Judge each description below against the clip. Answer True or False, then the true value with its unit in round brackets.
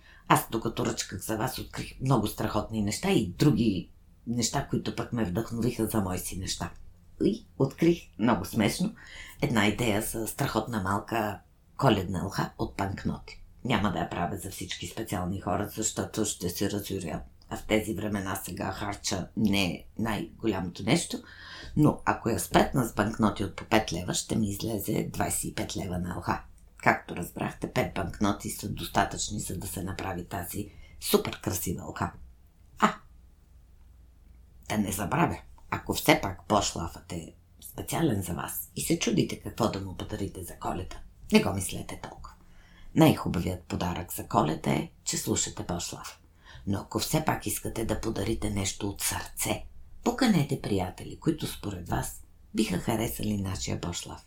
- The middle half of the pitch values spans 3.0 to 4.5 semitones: True (3.9 semitones)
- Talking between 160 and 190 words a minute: False (150 wpm)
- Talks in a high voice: False (100 Hz)